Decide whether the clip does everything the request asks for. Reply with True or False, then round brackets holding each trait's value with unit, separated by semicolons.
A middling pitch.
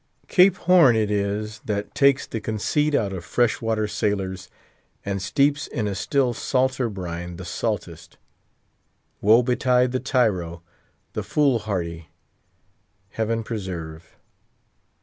False (110 Hz)